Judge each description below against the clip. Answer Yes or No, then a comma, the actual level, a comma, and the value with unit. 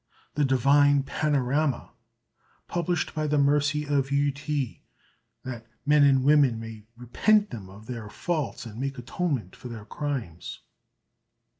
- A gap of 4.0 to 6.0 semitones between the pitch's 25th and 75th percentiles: No, average, 3.5 semitones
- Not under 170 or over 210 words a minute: No, slow, 135 wpm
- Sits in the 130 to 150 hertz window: Yes, medium, 140 Hz